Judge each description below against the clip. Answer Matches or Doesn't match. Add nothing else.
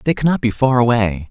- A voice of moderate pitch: Doesn't match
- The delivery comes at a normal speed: Doesn't match